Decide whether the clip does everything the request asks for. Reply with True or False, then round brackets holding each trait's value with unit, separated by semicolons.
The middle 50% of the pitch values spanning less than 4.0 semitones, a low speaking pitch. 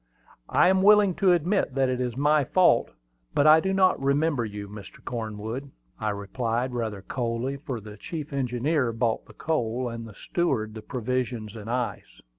False (5.0 semitones; 125 Hz)